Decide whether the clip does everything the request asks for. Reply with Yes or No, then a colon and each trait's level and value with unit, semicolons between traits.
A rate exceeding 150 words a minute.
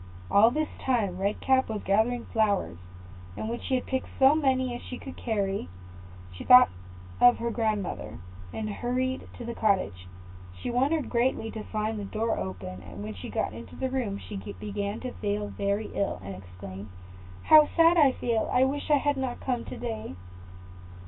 Yes: average, 180 wpm